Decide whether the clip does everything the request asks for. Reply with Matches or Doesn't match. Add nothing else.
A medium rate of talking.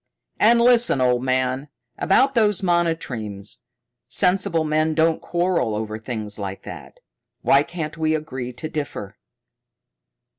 Doesn't match